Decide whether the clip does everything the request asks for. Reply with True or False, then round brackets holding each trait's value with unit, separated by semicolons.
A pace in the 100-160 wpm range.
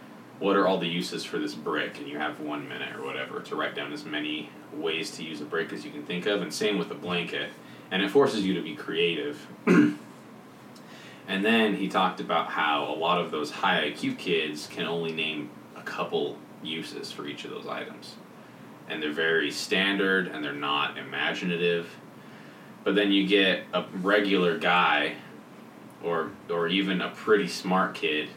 False (185 wpm)